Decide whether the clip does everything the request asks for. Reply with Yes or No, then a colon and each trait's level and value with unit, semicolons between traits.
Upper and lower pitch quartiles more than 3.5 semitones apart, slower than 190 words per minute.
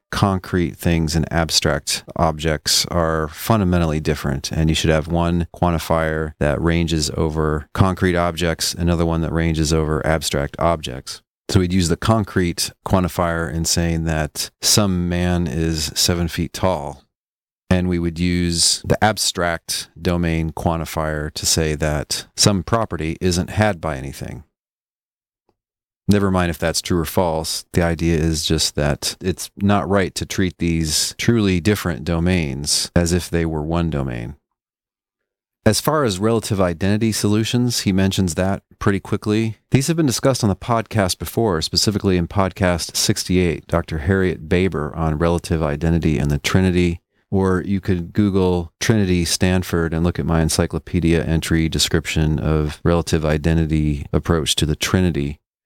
No: average, 3.0 semitones; average, 150 wpm